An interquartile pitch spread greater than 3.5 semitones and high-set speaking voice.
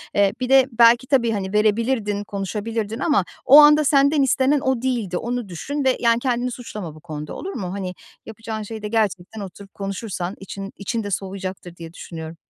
Yes: average, 4.3 semitones; high, 215 Hz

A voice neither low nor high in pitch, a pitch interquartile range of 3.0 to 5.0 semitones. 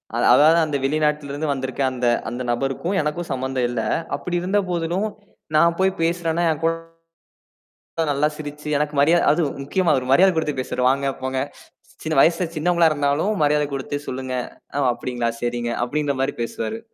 Yes: medium, 150 Hz; average, 4.0 semitones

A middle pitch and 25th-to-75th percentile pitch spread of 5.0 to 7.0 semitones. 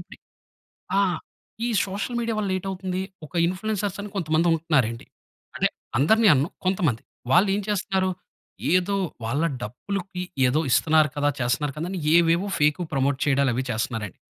Yes: medium, 165 Hz; wide, 5.6 semitones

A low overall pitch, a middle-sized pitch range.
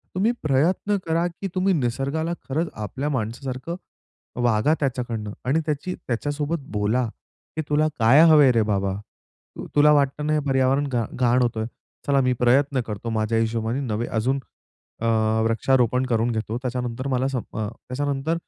Yes: low, 130 Hz; average, 4.1 semitones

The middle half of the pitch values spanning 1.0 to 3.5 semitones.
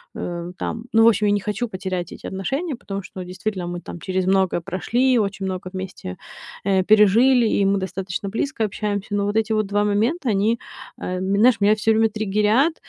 Yes: average, 2.8 semitones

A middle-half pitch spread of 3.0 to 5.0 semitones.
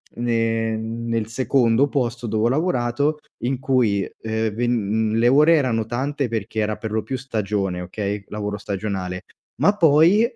Yes: average, 3.6 semitones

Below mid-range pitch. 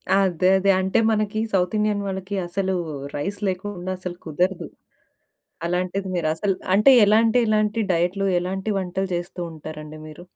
No: high, 190 Hz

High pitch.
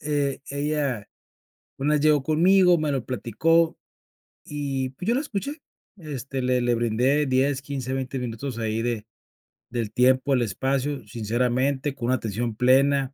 No: low, 135 Hz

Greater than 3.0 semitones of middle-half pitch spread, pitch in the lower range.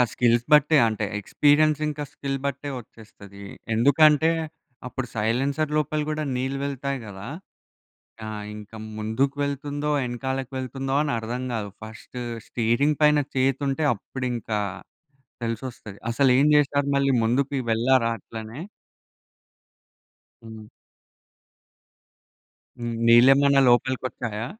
Yes: average, 3.7 semitones; low, 130 Hz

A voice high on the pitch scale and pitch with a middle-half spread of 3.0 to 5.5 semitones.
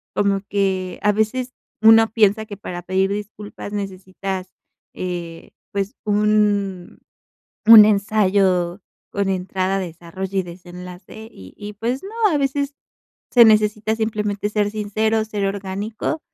No: high, 205 Hz; narrow, 2.4 semitones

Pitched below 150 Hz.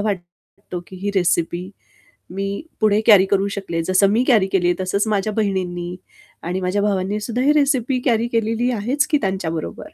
No: high, 200 Hz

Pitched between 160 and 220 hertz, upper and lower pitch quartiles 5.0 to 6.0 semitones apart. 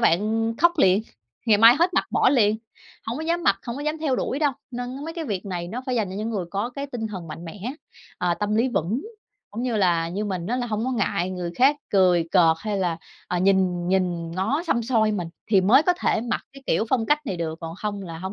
Yes: high, 210 Hz; average, 5.3 semitones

